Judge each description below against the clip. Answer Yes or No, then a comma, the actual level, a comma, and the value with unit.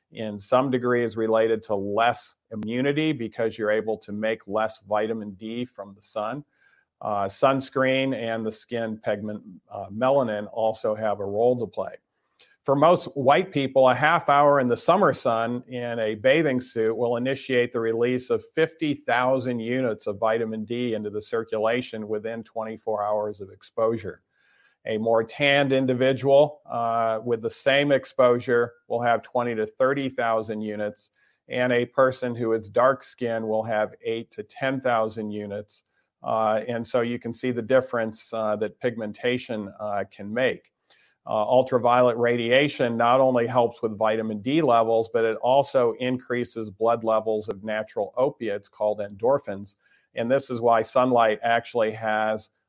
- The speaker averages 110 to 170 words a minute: Yes, average, 155 wpm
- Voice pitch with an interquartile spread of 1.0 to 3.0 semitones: Yes, average, 2.7 semitones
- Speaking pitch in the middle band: No, low, 115 Hz